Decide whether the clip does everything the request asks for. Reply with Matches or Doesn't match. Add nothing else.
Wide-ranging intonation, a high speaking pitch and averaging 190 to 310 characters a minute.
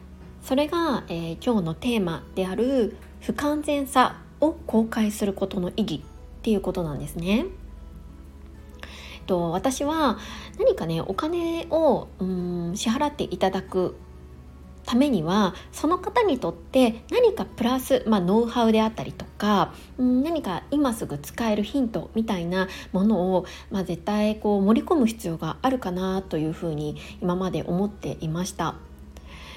Matches